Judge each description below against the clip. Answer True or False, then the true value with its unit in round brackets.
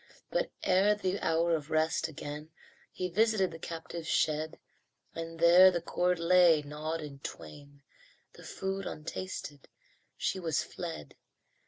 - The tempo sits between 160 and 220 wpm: False (135 wpm)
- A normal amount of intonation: True (3.0 semitones)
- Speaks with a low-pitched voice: False (165 Hz)